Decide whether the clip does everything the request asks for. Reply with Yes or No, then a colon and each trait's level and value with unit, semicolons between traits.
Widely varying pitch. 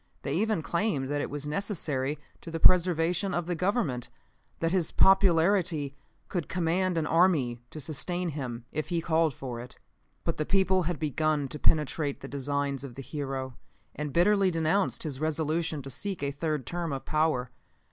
No: average, 3.9 semitones